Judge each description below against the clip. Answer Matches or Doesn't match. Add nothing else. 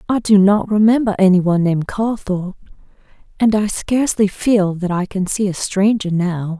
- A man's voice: Doesn't match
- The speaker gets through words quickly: Doesn't match